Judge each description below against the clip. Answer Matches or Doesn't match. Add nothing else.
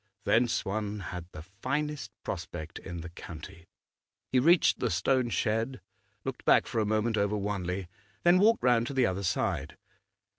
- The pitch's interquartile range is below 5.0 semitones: Doesn't match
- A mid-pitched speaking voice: Doesn't match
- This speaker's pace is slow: Doesn't match